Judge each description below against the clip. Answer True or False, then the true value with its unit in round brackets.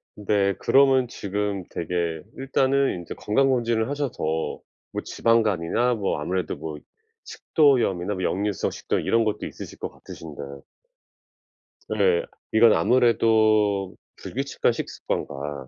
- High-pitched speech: False (105 Hz)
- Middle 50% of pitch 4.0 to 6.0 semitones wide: True (5.5 semitones)